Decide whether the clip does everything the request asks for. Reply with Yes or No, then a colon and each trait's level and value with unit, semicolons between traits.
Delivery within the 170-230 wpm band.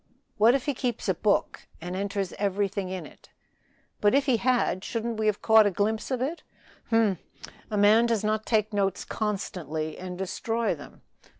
Yes: average, 180 wpm